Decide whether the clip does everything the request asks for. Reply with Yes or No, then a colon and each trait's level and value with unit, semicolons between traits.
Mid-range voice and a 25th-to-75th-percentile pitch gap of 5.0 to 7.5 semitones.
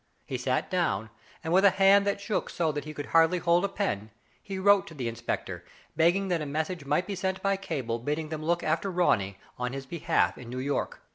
Yes: medium, 165 Hz; wide, 5.6 semitones